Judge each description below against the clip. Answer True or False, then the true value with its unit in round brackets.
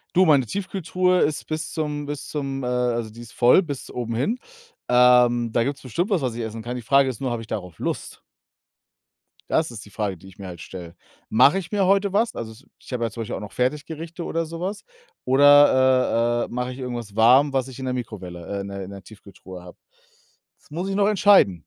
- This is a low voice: True (125 Hz)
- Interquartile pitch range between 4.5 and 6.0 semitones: True (5.6 semitones)